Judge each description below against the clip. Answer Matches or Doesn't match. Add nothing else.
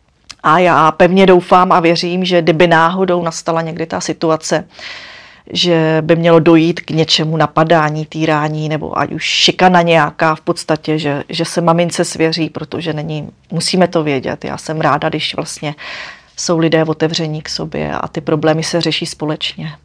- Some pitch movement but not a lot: Doesn't match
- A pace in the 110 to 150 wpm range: Doesn't match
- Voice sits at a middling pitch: Matches